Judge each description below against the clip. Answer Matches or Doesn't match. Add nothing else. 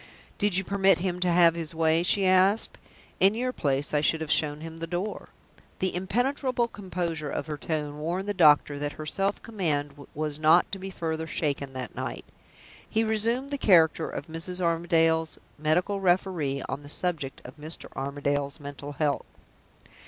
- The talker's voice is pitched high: Doesn't match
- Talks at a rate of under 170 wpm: Doesn't match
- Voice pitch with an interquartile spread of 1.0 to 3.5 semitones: Doesn't match